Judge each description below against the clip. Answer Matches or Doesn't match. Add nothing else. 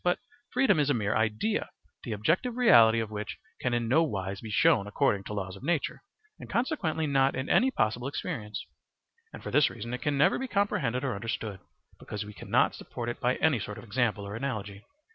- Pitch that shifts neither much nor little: Doesn't match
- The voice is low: Matches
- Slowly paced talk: Doesn't match